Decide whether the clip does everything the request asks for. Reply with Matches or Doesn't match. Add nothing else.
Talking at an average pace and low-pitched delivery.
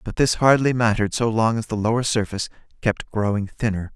Matches